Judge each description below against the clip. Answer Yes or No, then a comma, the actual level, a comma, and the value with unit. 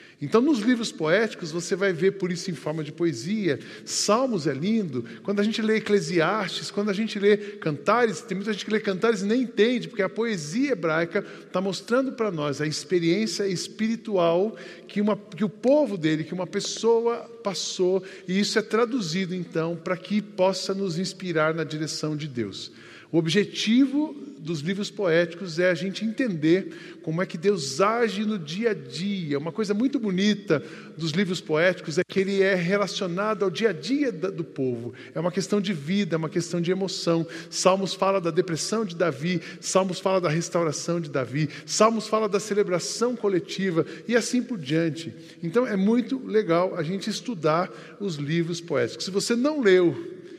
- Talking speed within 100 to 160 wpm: No, average, 180 wpm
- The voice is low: No, high, 190 Hz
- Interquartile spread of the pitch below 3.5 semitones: No, average, 4.0 semitones